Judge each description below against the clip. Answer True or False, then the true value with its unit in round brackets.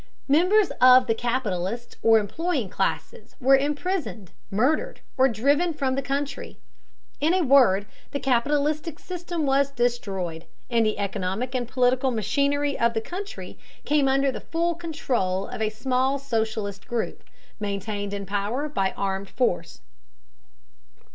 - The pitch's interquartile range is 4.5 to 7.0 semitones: True (5.1 semitones)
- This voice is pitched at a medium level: False (255 Hz)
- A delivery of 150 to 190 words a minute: False (135 wpm)